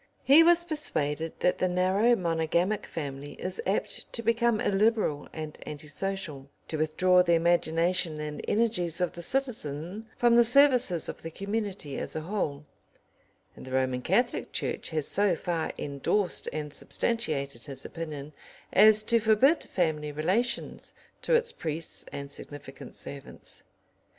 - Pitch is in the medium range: Yes, medium, 175 Hz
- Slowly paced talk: No, average, 145 wpm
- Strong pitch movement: Yes, wide, 6.2 semitones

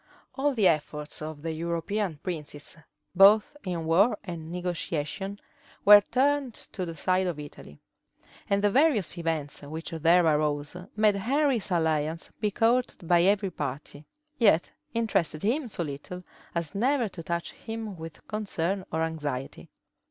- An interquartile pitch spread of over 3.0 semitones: Yes, average, 4.8 semitones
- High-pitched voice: No, medium, 175 Hz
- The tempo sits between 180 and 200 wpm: No, average, 145 wpm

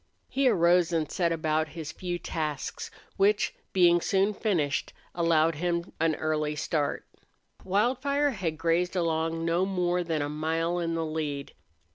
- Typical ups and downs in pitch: No, narrow, 2.3 semitones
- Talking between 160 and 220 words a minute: No, average, 145 wpm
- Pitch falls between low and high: Yes, medium, 165 Hz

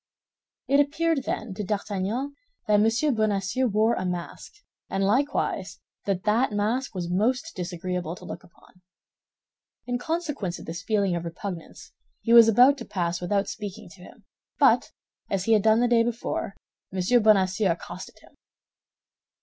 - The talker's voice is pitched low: No, high, 210 Hz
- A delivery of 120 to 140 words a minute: No, average, 155 wpm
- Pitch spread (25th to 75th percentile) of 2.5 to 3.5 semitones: No, average, 4.4 semitones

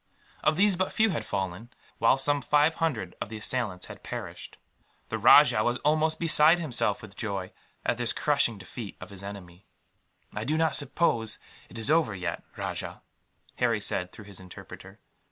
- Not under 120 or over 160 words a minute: No, average, 170 wpm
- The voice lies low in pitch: Yes, low, 120 Hz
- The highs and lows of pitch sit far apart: Yes, wide, 7.5 semitones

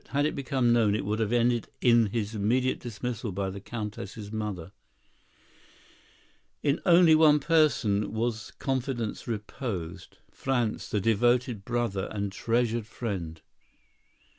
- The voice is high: No, low, 115 Hz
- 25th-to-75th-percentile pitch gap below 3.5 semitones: Yes, average, 3.1 semitones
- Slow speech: Yes, slow, 125 wpm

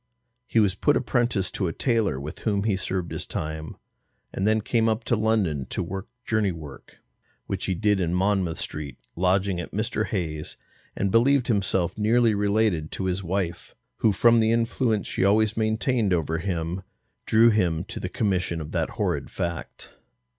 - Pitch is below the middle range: Yes, low, 100 Hz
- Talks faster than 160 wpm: Yes, average, 175 wpm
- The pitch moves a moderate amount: Yes, average, 4.1 semitones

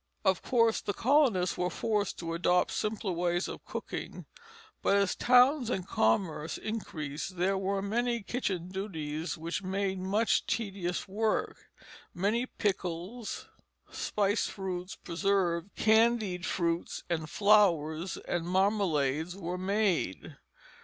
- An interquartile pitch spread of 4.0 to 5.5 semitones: No, average, 3.5 semitones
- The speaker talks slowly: Yes, slow, 120 wpm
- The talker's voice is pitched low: No, high, 190 Hz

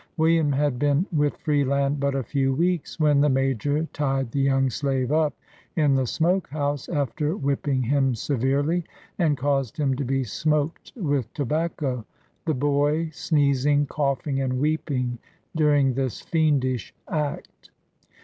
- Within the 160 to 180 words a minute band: No, average, 145 wpm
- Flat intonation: Yes, narrow, 2.2 semitones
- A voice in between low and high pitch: Yes, medium, 145 Hz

